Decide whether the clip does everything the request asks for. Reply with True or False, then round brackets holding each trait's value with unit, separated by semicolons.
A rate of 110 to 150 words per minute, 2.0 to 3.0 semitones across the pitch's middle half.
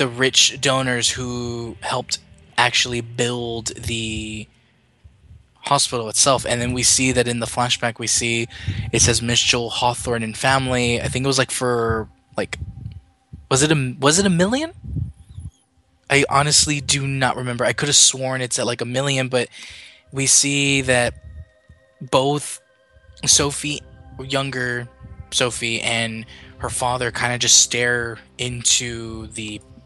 True (145 wpm; 2.4 semitones)